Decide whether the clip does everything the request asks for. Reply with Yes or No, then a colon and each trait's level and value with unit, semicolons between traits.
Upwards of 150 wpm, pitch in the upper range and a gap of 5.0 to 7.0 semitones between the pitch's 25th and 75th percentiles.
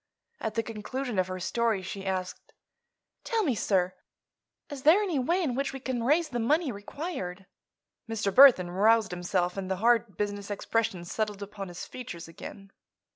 Yes: average, 170 wpm; high, 215 Hz; average, 5.3 semitones